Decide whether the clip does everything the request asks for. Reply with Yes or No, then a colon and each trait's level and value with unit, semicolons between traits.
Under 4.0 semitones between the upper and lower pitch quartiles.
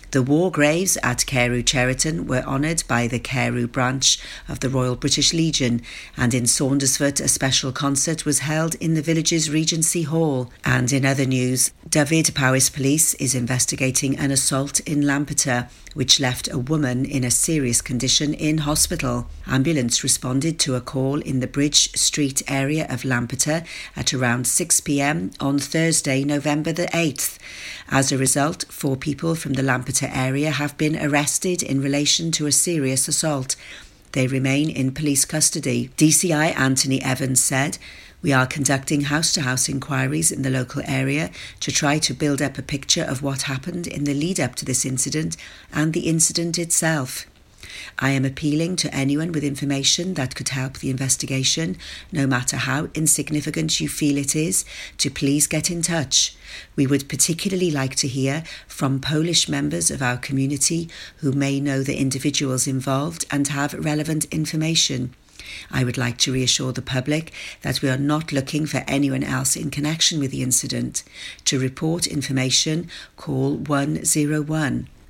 Yes: average, 2.7 semitones